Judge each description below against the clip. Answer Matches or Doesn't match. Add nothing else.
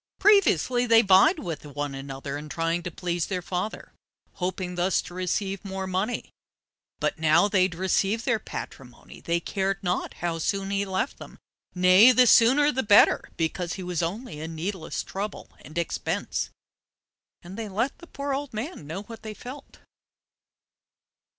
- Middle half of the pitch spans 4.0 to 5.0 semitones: Matches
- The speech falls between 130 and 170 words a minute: Matches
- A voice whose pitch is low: Doesn't match